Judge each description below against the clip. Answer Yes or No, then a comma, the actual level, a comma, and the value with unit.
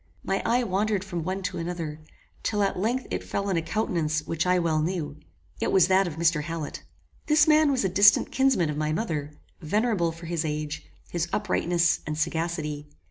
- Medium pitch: Yes, medium, 170 Hz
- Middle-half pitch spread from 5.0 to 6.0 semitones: No, average, 4.1 semitones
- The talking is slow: No, average, 190 wpm